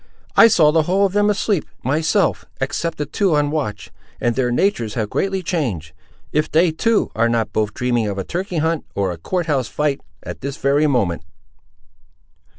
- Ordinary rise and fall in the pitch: No, wide, 6.9 semitones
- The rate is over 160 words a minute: Yes, average, 185 wpm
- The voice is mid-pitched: Yes, medium, 150 Hz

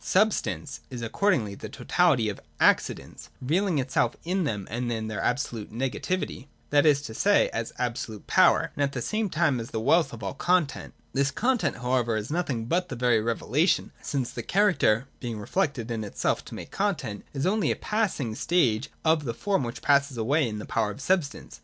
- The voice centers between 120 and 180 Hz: Yes, low, 135 Hz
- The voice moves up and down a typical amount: No, wide, 6.9 semitones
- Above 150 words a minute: Yes, average, 200 wpm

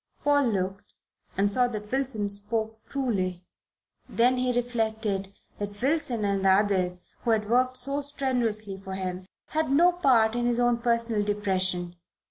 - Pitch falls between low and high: No, high, 220 Hz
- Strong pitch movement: No, average, 4.0 semitones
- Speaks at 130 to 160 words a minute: Yes, average, 150 wpm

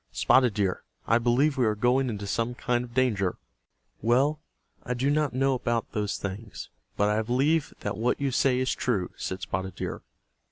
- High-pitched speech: No, low, 120 Hz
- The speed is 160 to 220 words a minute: Yes, average, 185 wpm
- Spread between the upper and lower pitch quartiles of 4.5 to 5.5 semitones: No, average, 3.7 semitones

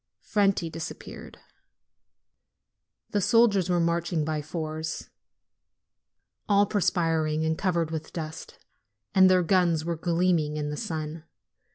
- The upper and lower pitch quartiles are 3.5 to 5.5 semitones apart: No, narrow, 2.6 semitones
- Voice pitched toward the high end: No, medium, 165 Hz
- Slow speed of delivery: Yes, slow, 110 wpm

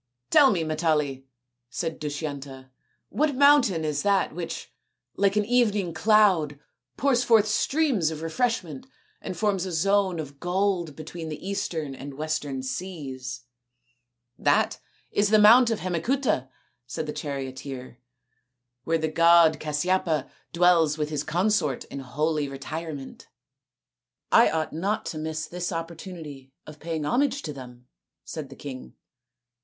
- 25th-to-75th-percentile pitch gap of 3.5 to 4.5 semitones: No, average, 5.3 semitones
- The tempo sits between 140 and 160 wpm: Yes, average, 145 wpm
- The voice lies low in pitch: No, medium, 160 Hz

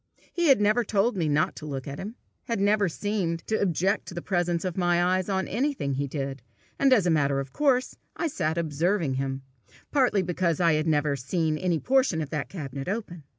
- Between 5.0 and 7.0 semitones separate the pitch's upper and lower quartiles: Yes, wide, 5.4 semitones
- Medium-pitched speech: Yes, medium, 175 Hz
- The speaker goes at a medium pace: No, fast, 210 wpm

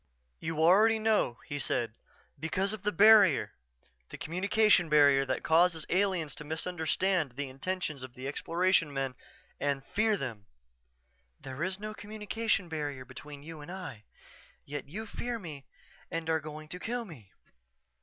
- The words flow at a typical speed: Yes, average, 150 wpm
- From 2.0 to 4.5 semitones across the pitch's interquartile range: No, wide, 5.5 semitones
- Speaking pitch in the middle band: Yes, medium, 160 Hz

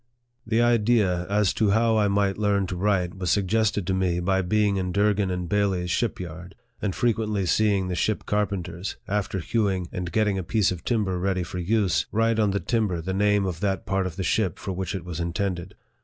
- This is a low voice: Yes, very low, 95 Hz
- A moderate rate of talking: No, fast, 215 wpm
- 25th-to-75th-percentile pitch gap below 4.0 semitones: Yes, narrow, 2.6 semitones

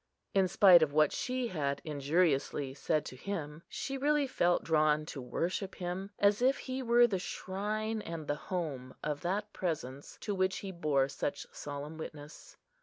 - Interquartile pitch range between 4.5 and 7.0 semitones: Yes, wide, 5.6 semitones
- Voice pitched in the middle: Yes, medium, 170 Hz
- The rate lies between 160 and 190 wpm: Yes, average, 170 wpm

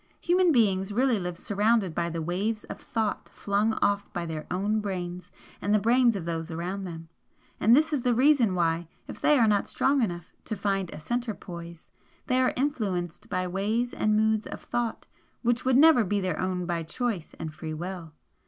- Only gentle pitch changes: No, average, 5.1 semitones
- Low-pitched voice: No, high, 200 Hz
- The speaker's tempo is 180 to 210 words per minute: Yes, average, 195 wpm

